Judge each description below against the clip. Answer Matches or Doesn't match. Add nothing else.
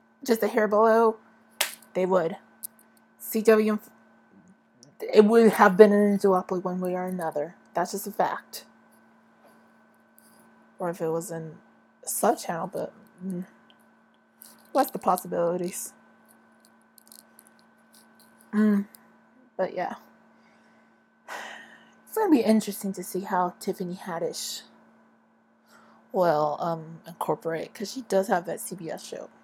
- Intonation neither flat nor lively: Matches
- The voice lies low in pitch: Doesn't match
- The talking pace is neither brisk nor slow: Doesn't match